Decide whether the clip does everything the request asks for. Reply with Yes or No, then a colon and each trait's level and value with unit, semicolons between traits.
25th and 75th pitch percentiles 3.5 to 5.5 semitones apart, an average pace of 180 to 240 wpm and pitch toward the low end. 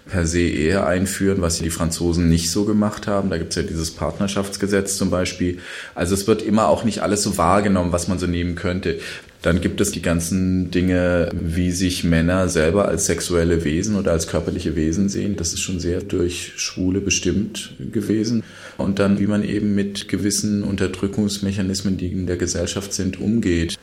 No: narrow, 2.5 semitones; average, 185 wpm; very low, 95 Hz